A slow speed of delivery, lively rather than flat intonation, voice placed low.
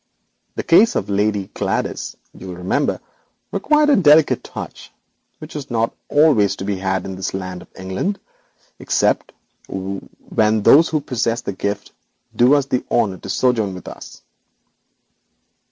No: average, 150 wpm; wide, 7.3 semitones; low, 110 Hz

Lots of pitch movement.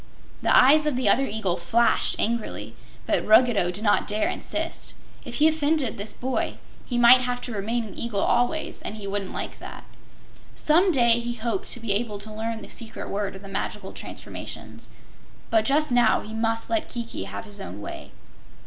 No: average, 3.2 semitones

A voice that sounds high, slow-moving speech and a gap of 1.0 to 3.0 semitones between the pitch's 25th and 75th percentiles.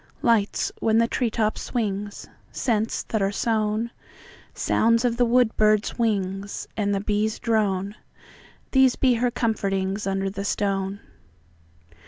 Yes: high, 215 Hz; slow, 110 wpm; narrow, 2.5 semitones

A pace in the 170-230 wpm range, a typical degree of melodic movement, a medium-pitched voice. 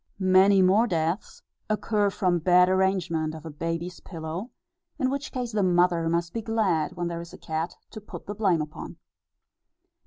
Yes: average, 175 wpm; average, 3.6 semitones; medium, 180 Hz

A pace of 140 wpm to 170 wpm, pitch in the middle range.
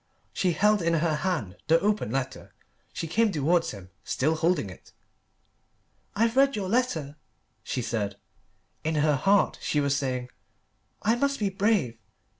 Yes: average, 150 wpm; medium, 165 Hz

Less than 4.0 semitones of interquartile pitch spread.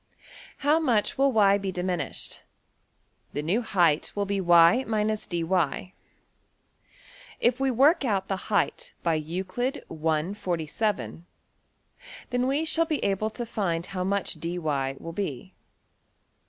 No: average, 5.2 semitones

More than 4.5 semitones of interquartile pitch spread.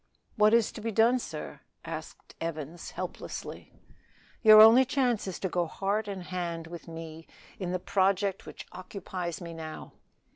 No: average, 4.2 semitones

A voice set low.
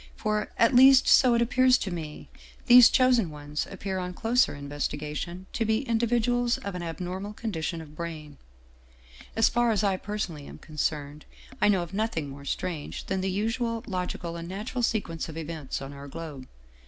No: medium, 185 Hz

